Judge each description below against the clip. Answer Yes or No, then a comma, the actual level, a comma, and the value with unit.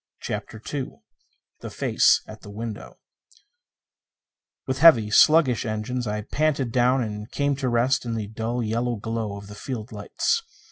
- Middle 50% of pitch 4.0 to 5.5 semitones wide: No, average, 3.4 semitones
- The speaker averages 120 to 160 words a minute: Yes, average, 150 wpm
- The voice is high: No, low, 115 Hz